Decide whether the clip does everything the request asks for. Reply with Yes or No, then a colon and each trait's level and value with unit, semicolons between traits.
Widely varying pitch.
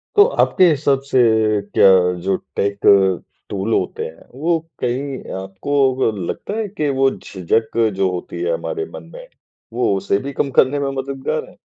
Yes: wide, 7.1 semitones